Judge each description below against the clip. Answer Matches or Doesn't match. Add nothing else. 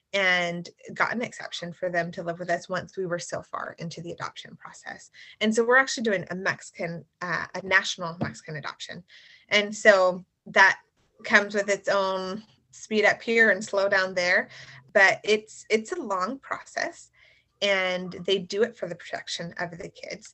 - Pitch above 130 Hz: Matches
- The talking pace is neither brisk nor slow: Matches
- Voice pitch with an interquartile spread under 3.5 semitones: Matches